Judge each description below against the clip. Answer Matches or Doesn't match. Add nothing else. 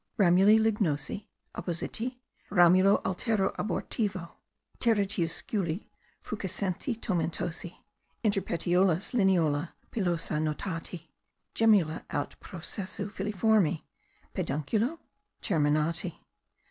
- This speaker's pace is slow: Matches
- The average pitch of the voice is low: Doesn't match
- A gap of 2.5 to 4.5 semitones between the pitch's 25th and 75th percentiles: Matches